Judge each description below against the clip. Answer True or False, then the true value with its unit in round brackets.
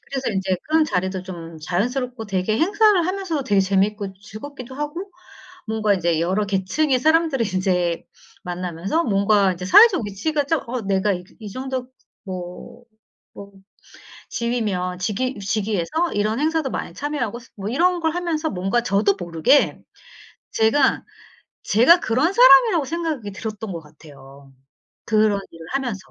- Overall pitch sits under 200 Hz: False (220 Hz)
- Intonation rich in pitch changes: True (7.4 semitones)